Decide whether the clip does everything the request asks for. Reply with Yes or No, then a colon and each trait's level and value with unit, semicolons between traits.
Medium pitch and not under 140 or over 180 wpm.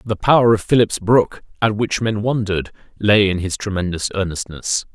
No: low, 105 Hz; average, 170 wpm